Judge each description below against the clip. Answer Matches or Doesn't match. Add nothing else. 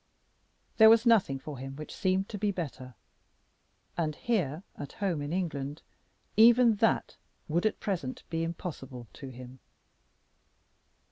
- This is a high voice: Doesn't match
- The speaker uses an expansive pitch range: Matches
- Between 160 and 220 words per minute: Doesn't match